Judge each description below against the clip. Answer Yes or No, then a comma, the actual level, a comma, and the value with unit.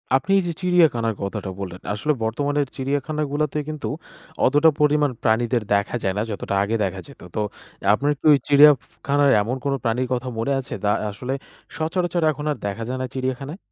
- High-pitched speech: No, low, 135 Hz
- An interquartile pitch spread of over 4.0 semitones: Yes, average, 4.6 semitones